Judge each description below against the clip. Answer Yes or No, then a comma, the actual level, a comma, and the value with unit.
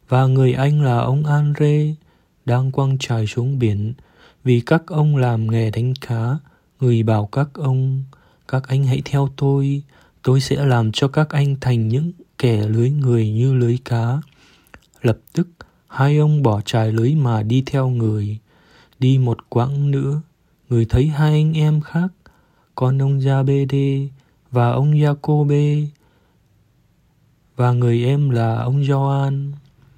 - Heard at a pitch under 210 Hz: Yes, low, 135 Hz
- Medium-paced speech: No, slow, 150 wpm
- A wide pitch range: No, average, 2.9 semitones